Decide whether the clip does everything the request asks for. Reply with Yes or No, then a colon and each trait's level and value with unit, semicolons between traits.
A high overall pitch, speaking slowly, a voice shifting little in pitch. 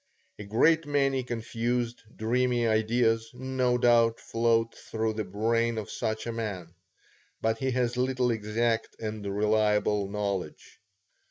No: low, 115 Hz; slow, 125 wpm; narrow, 2.1 semitones